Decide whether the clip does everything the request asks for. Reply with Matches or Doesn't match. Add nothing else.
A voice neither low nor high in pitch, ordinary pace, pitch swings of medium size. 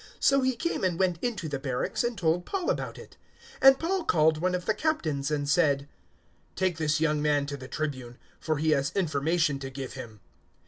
Doesn't match